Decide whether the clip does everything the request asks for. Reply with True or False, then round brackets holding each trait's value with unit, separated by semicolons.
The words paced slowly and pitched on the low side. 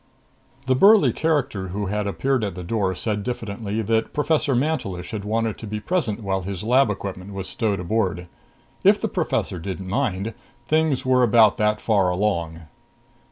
False (170 wpm; 105 Hz)